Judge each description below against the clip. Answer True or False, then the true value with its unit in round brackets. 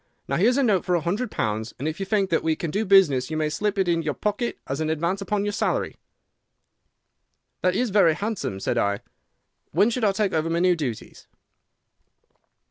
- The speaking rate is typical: False (215 wpm)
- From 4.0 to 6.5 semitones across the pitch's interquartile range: True (4.7 semitones)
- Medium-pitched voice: True (180 Hz)